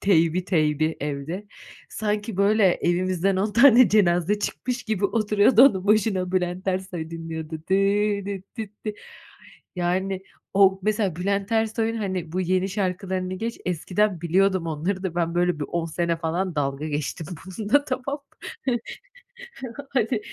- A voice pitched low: No, high, 190 Hz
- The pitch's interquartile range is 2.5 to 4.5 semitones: Yes, average, 3.3 semitones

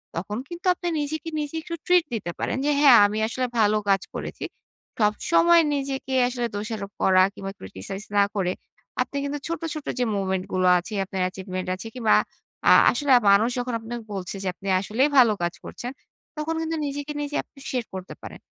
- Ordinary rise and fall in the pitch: No, wide, 6.7 semitones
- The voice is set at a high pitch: Yes, high, 230 Hz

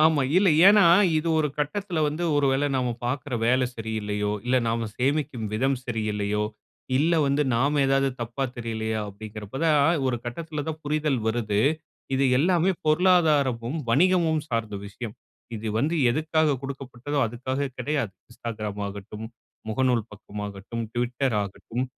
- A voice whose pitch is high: No, low, 130 Hz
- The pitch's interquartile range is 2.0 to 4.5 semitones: No, average, 5.1 semitones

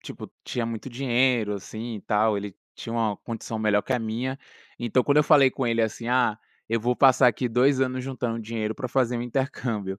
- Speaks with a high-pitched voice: No, low, 120 Hz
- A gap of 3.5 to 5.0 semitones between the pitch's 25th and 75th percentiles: No, narrow, 2.6 semitones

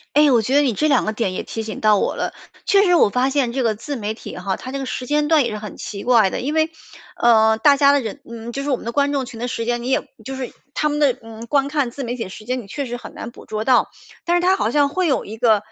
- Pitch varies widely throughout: No, average, 4.2 semitones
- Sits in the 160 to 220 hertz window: No, very high, 250 Hz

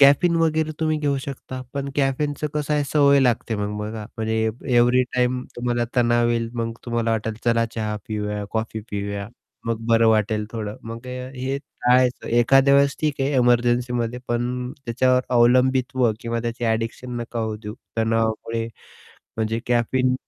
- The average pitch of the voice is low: Yes, low, 120 Hz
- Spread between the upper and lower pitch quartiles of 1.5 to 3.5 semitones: Yes, narrow, 2.4 semitones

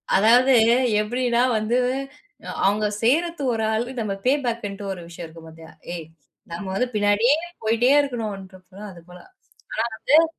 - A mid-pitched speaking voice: No, high, 215 Hz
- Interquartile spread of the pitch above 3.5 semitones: Yes, average, 4.3 semitones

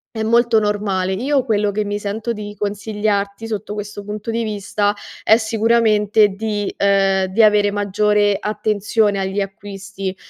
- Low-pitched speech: No, high, 210 Hz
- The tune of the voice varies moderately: No, narrow, 1.4 semitones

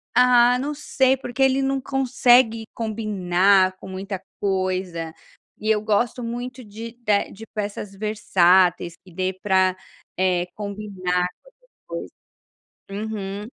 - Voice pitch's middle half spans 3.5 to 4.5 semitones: Yes, average, 4.2 semitones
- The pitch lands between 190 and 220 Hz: Yes, high, 210 Hz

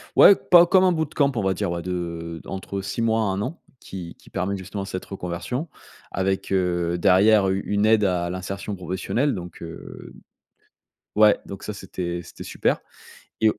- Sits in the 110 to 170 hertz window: No, very low, 95 Hz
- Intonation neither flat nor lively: Yes, average, 3.2 semitones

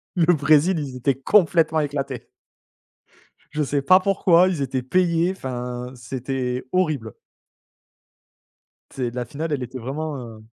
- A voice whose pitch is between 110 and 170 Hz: Yes, medium, 140 Hz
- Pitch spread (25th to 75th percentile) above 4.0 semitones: Yes, average, 4.6 semitones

